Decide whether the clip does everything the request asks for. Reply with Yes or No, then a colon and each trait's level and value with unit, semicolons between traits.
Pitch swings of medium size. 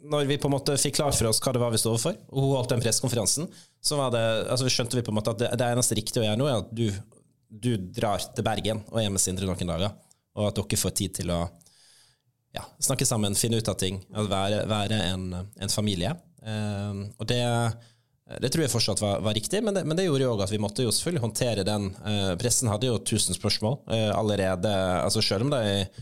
Yes: average, 3.8 semitones